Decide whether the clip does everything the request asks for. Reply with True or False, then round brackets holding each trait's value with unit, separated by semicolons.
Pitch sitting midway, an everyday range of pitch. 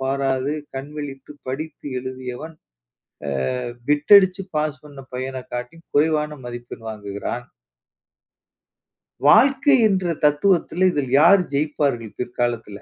True (145 Hz; 3.8 semitones)